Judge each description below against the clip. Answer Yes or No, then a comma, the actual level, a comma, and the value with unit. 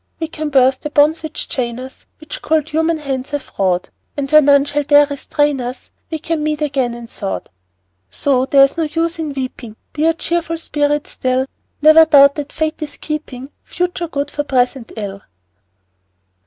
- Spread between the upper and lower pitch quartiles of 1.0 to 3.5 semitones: Yes, average, 3.0 semitones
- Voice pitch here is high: Yes, very high, 290 Hz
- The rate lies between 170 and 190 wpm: Yes, average, 180 wpm